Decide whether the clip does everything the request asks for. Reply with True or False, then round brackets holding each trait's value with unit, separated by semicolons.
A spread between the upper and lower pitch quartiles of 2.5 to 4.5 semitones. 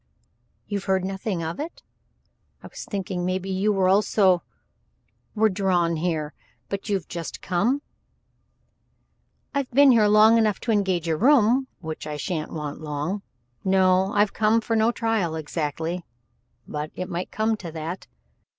True (4.2 semitones)